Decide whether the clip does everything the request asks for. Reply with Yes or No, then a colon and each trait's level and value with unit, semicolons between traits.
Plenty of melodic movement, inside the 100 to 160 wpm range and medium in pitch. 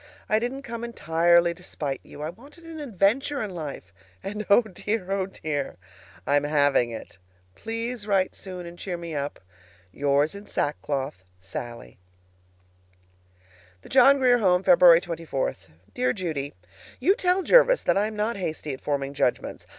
Yes: wide, 7.6 semitones; average, 155 wpm; medium, 180 Hz